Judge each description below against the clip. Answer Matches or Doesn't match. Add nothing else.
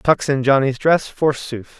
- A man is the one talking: Matches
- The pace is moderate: Matches